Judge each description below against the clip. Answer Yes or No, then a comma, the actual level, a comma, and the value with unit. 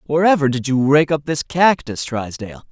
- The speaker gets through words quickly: No, average, 175 wpm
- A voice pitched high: No, medium, 140 Hz